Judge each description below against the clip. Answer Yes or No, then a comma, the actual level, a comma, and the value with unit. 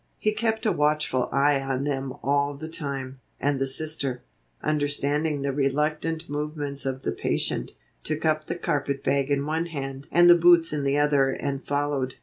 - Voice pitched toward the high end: No, medium, 145 Hz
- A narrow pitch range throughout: Yes, narrow, 2.0 semitones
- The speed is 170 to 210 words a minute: Yes, average, 175 wpm